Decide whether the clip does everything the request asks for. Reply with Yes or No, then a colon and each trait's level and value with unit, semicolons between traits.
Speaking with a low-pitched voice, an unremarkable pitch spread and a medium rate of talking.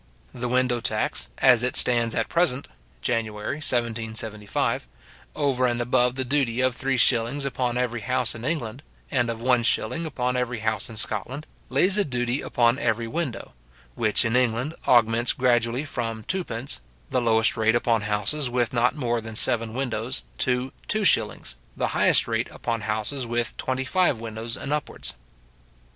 No: low, 120 Hz; narrow, 2.3 semitones; average, 160 wpm